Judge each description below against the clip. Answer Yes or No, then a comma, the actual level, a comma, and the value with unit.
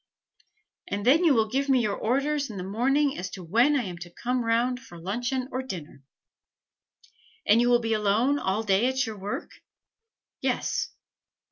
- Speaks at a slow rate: No, average, 175 wpm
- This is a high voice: Yes, high, 235 Hz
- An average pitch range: Yes, average, 4.6 semitones